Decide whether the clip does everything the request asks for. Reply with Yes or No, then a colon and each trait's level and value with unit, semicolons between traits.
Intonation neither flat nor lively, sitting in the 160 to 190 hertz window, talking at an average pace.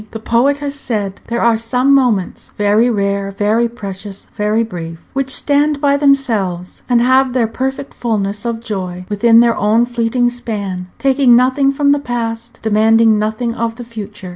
No: average, 3.4 semitones; high, 230 Hz; average, 165 wpm